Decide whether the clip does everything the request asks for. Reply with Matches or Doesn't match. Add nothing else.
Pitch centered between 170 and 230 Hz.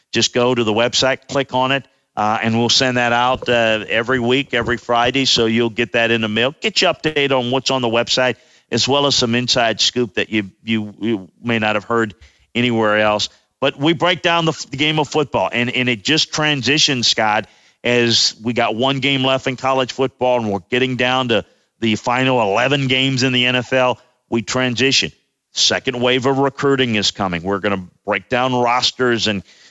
Doesn't match